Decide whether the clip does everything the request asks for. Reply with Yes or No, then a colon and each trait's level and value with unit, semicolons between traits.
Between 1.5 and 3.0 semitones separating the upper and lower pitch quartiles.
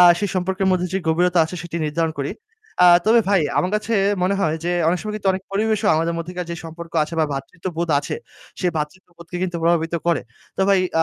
Yes: narrow, 2.4 semitones